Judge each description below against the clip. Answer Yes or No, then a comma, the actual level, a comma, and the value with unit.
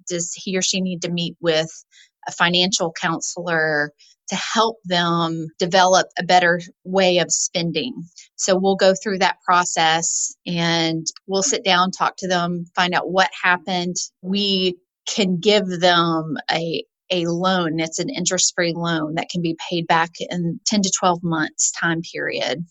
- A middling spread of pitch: No, narrow, 1.8 semitones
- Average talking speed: Yes, average, 160 wpm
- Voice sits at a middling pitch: Yes, medium, 180 Hz